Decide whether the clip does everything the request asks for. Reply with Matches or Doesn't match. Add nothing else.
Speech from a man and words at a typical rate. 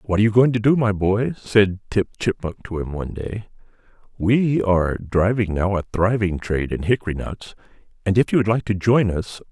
Doesn't match